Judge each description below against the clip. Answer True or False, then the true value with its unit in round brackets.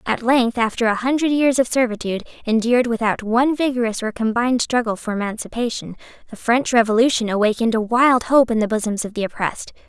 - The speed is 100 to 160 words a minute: False (180 wpm)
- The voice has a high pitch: True (230 Hz)